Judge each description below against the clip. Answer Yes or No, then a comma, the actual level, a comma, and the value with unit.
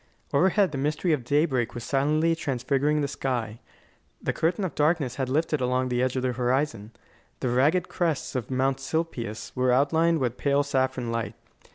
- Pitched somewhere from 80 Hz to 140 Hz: Yes, low, 135 Hz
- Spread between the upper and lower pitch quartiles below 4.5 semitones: Yes, average, 3.2 semitones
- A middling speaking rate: Yes, average, 175 wpm